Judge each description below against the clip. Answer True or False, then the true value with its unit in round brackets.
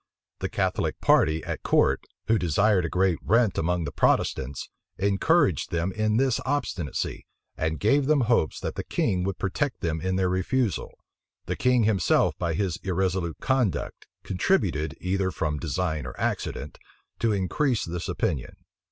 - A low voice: True (95 Hz)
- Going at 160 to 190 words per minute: False (150 wpm)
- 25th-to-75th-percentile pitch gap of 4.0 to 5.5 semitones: True (5.1 semitones)